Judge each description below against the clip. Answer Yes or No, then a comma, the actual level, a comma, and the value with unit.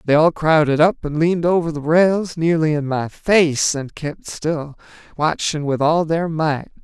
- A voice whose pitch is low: No, medium, 155 Hz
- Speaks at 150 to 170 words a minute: No, average, 185 wpm